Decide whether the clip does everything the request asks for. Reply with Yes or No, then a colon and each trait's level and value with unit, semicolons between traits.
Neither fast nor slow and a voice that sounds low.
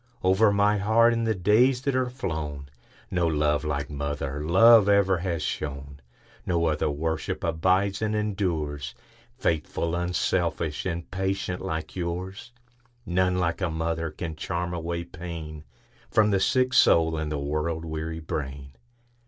No: slow, 130 wpm; very low, 85 Hz